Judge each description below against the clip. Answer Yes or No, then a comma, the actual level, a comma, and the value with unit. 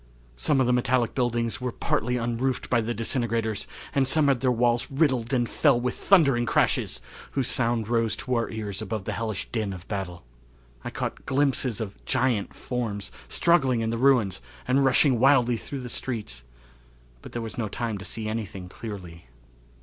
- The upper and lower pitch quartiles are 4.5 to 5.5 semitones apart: No, average, 2.9 semitones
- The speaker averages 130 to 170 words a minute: No, average, 180 wpm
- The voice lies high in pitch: No, low, 120 Hz